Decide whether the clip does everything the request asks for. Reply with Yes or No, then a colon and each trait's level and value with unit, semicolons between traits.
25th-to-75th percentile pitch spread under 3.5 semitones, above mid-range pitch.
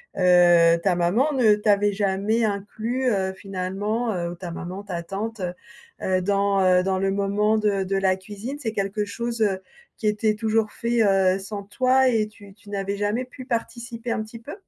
Yes: average, 2.8 semitones; high, 205 Hz